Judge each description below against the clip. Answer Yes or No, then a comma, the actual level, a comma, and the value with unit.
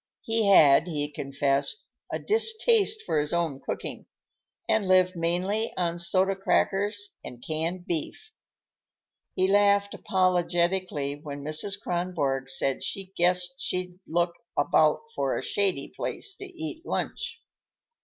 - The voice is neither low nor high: Yes, medium, 180 Hz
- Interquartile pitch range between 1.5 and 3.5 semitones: No, average, 4.4 semitones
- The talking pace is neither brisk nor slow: No, slow, 125 wpm